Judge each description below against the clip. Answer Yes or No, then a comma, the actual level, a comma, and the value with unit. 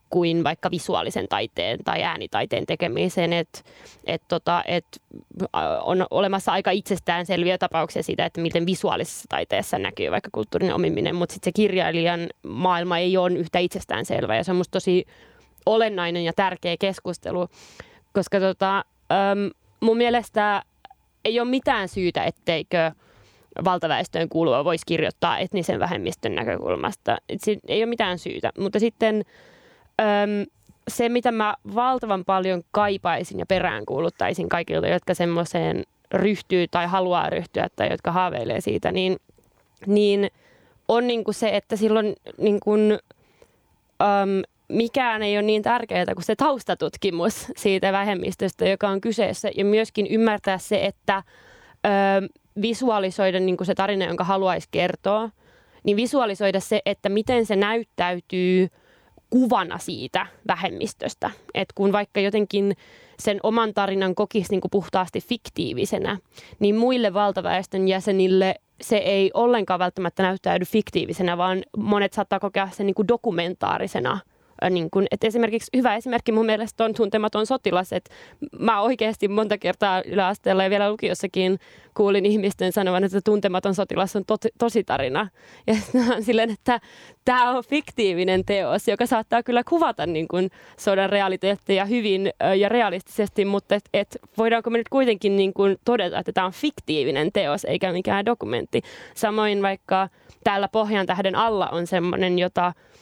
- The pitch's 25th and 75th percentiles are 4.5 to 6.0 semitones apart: No, average, 2.8 semitones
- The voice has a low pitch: No, high, 200 Hz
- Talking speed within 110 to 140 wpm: Yes, average, 135 wpm